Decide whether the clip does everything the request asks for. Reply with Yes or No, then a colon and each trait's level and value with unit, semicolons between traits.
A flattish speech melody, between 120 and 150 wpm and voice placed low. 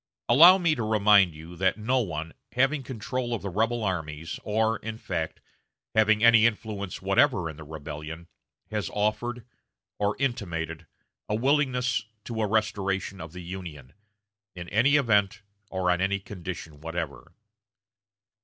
No: average, 5.1 semitones; average, 145 wpm; low, 105 Hz